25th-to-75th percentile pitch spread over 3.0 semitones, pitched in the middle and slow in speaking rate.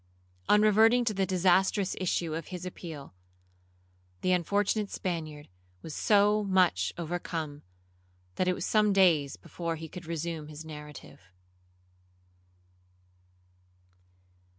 Yes: average, 3.7 semitones; medium, 175 Hz; slow, 110 wpm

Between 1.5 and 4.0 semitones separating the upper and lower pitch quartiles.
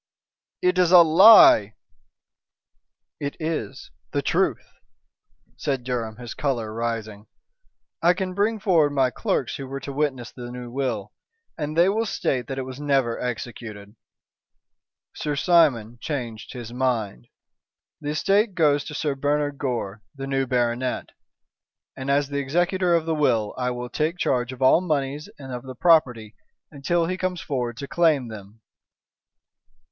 No: average, 4.6 semitones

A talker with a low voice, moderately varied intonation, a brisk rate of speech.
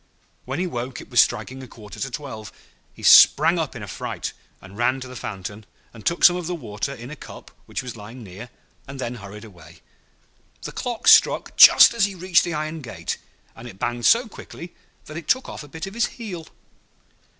No: low, 130 Hz; wide, 7.2 semitones; fast, 215 wpm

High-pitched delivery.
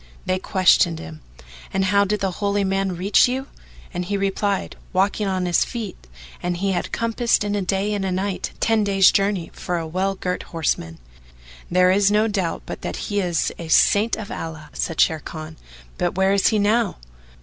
Yes: high, 195 Hz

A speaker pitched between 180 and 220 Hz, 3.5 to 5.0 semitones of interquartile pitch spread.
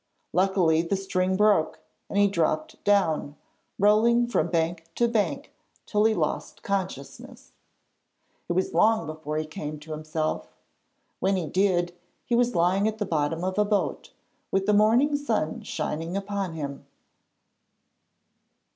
Yes: high, 190 Hz; average, 4.5 semitones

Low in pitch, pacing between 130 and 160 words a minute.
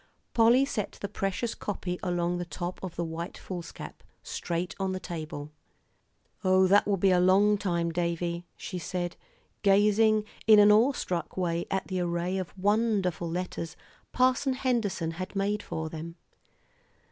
No: medium, 185 Hz; average, 155 wpm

